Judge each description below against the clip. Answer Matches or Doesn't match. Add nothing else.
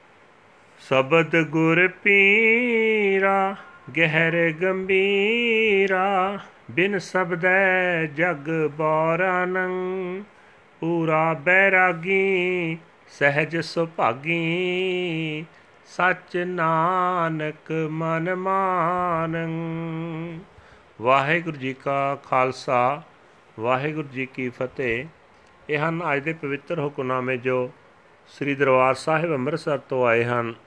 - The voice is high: Doesn't match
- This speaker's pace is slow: Matches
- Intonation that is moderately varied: Matches